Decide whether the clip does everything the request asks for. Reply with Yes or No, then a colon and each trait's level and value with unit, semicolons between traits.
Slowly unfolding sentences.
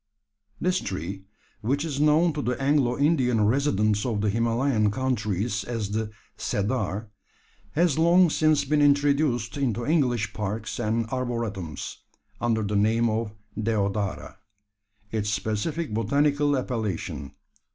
Yes: slow, 120 wpm